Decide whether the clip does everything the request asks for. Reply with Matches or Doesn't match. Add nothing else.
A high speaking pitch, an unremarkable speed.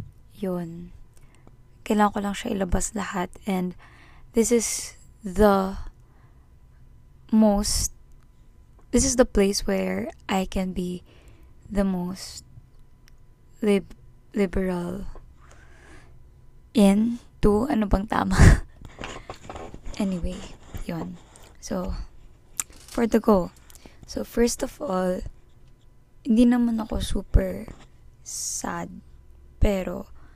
Doesn't match